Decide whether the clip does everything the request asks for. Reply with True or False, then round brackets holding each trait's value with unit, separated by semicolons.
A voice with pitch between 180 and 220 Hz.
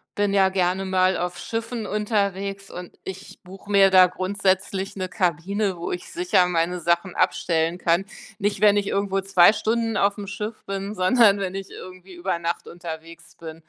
True (190 Hz)